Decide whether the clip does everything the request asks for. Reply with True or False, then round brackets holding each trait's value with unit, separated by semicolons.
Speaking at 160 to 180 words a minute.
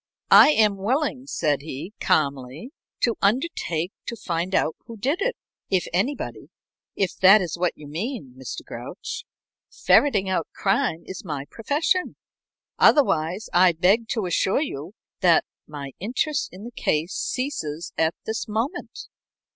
False (140 wpm)